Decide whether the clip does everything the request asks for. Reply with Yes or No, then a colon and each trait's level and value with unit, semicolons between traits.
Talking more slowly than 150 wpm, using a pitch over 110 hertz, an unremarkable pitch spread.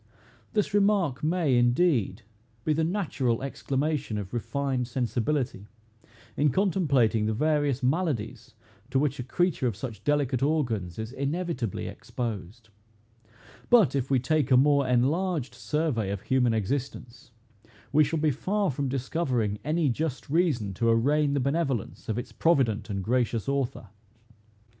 Yes: average, 140 wpm; low, 135 Hz; average, 4.6 semitones